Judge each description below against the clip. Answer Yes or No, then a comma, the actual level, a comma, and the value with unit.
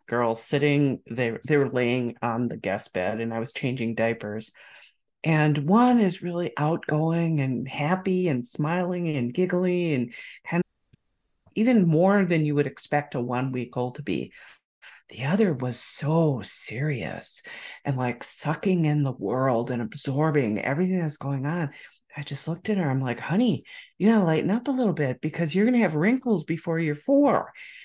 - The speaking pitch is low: No, medium, 150 Hz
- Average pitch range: No, wide, 6.1 semitones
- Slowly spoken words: No, average, 170 wpm